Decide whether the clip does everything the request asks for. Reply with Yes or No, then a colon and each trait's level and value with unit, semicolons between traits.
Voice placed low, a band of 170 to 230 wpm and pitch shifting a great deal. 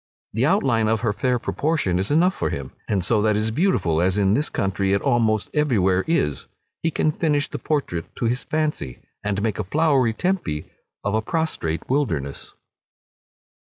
Yes: low, 110 Hz; average, 180 wpm; wide, 7.5 semitones